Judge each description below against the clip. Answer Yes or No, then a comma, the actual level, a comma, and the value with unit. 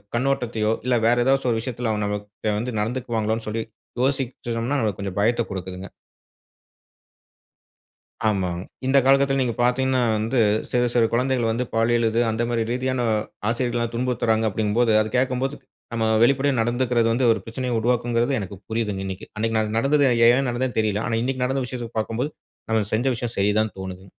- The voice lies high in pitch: No, low, 120 Hz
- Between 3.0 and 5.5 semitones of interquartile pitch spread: No, narrow, 2.5 semitones